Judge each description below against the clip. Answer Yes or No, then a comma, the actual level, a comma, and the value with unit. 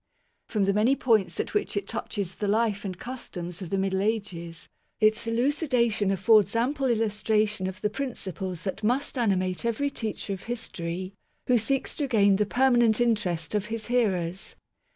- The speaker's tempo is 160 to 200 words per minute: Yes, average, 170 wpm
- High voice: Yes, high, 210 Hz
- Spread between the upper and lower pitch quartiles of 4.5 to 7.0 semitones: No, average, 3.6 semitones